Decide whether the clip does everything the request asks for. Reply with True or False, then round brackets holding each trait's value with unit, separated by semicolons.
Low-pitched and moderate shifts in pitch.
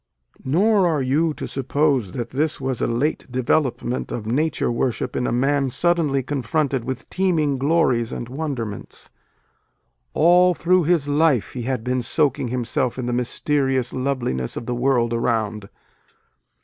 True (130 Hz; 4.0 semitones)